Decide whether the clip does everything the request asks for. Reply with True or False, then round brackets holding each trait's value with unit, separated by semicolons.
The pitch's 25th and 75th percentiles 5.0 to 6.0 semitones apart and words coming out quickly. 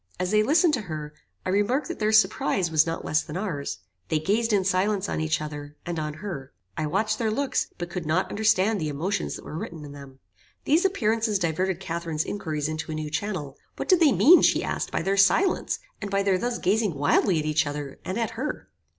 True (5.6 semitones; 220 wpm)